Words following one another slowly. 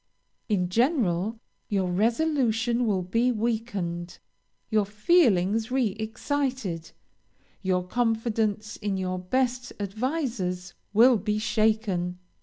Yes: slow, 95 wpm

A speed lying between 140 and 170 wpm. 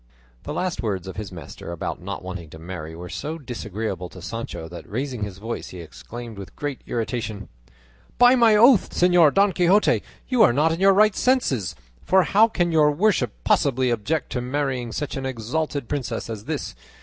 No: average, 185 wpm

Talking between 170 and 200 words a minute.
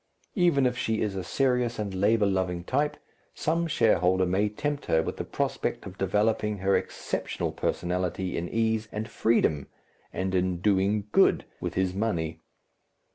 No: average, 155 wpm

